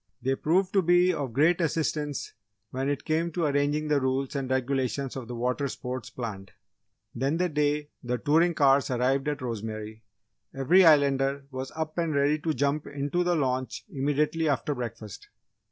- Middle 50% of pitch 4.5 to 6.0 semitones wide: No, average, 2.9 semitones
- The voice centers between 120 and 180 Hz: Yes, medium, 140 Hz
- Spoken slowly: No, average, 170 wpm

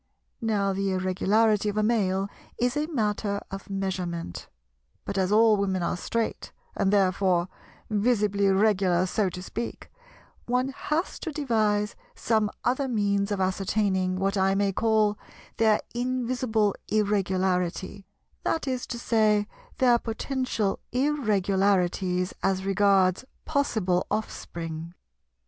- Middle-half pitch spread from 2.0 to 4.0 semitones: Yes, average, 3.0 semitones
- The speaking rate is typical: No, slow, 120 wpm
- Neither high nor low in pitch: No, high, 205 Hz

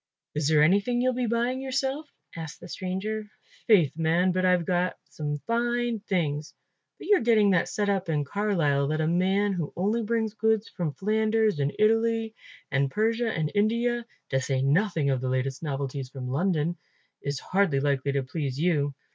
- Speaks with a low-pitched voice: No, medium, 185 Hz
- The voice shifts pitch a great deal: Yes, wide, 7.0 semitones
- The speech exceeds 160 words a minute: Yes, average, 170 wpm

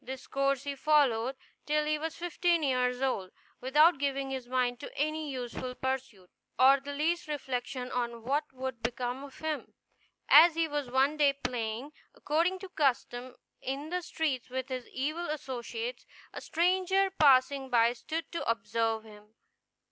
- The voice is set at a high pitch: Yes, very high, 270 Hz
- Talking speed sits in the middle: Yes, average, 155 wpm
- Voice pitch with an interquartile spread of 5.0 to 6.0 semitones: No, average, 3.6 semitones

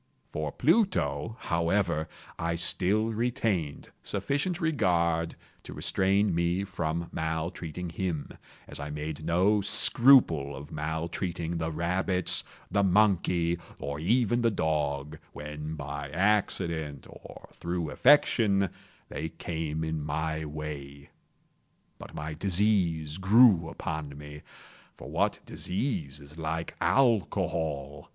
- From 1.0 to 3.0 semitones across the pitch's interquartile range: No, average, 4.4 semitones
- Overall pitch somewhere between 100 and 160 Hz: No, very low, 85 Hz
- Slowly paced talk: Yes, slow, 110 wpm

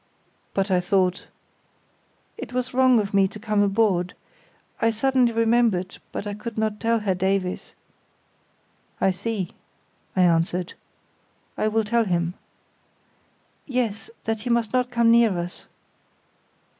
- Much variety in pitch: No, average, 3.7 semitones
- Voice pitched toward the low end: No, high, 210 Hz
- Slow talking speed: Yes, slow, 130 wpm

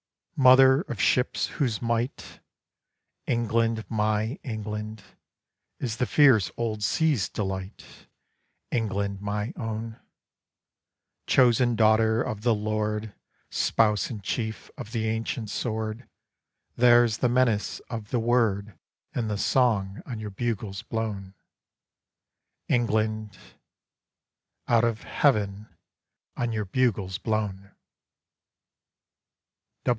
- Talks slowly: Yes, slow, 100 wpm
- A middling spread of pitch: No, narrow, 2.2 semitones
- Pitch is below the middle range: Yes, low, 110 Hz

